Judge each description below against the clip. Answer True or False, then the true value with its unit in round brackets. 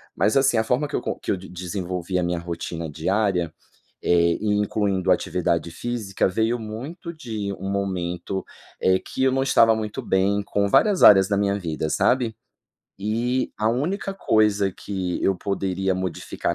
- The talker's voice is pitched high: False (100 Hz)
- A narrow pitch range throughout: False (3.6 semitones)